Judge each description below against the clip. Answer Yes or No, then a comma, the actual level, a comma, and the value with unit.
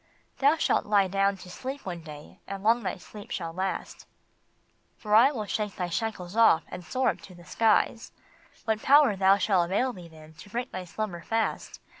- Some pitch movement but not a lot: Yes, average, 4.2 semitones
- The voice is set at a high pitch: Yes, high, 200 Hz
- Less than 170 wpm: No, average, 190 wpm